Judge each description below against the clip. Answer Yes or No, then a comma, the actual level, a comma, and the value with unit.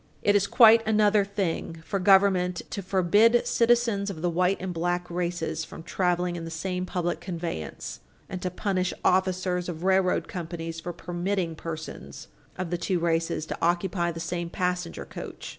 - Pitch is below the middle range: No, medium, 180 Hz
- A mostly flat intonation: Yes, narrow, 2.0 semitones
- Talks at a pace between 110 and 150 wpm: No, average, 165 wpm